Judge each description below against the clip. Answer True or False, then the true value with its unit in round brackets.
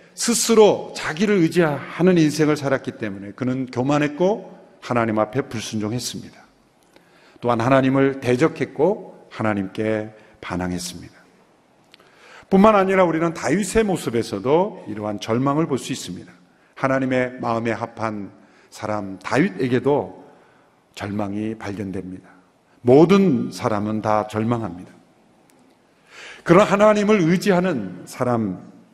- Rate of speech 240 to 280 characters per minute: True (275 characters per minute)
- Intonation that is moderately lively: False (7.5 semitones)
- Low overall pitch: True (125 Hz)